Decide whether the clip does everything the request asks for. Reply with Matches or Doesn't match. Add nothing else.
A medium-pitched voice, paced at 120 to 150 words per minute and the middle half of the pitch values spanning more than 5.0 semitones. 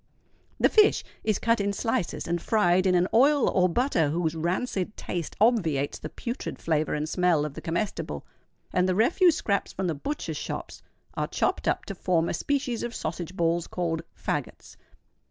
Doesn't match